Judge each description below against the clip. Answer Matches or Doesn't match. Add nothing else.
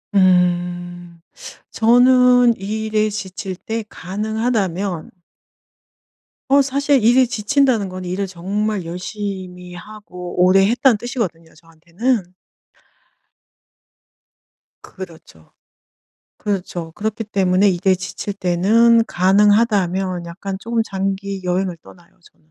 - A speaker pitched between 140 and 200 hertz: Matches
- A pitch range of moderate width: Matches